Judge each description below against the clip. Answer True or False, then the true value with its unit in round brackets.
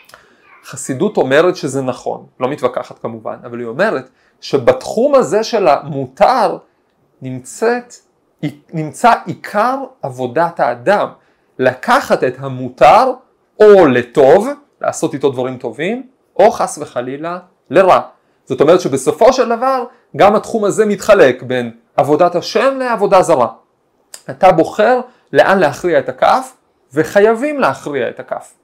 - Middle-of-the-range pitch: True (180 Hz)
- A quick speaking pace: False (115 wpm)